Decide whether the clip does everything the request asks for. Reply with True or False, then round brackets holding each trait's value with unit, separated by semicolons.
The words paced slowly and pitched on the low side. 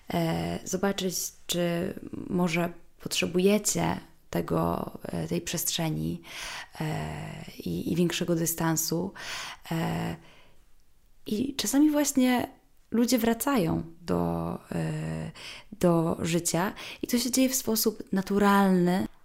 False (80 wpm; 180 Hz)